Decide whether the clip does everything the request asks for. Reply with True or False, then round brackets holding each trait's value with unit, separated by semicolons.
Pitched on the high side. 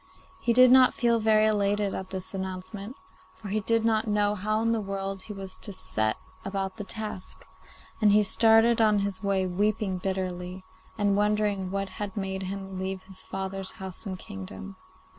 True (195 Hz)